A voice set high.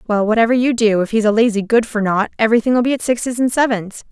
Yes: high, 225 Hz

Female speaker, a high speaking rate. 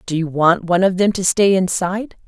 Yes: female; fast, 240 wpm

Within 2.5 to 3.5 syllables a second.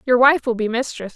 No: 5.8 syllables/s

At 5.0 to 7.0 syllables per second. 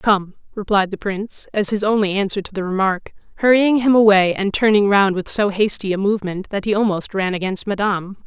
Yes: 5.6 syllables/s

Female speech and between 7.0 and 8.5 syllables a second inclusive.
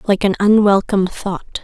No: female; 4.8 syllables/s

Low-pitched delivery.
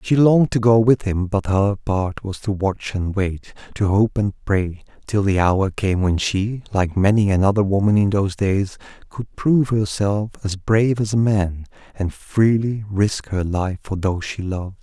Yes: low, 100 Hz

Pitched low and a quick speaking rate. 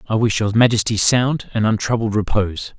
No: low, 110 Hz; average, 175 wpm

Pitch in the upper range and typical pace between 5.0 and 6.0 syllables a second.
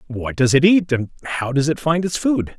No: medium, 145 Hz; 5.2 syllables/s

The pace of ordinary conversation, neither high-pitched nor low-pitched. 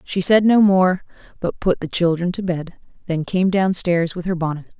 No: fast, 215 wpm; medium, 180 Hz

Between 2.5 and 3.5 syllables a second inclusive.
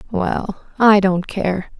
Yes: 3.0 syllables/s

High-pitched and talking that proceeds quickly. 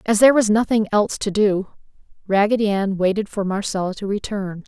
No: high, 205 Hz; average, 180 wpm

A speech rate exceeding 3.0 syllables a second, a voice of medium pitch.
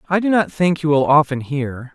Yes: 5.1 syllables/s; medium, 155 Hz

